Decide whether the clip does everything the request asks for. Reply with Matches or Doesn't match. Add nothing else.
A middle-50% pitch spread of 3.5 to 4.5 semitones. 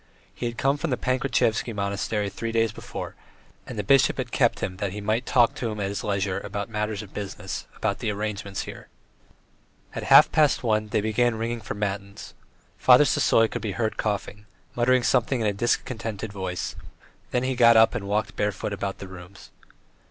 Doesn't match